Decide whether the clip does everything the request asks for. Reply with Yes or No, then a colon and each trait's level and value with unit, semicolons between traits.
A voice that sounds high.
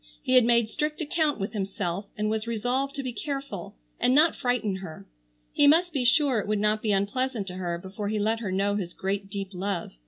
Yes: high, 215 Hz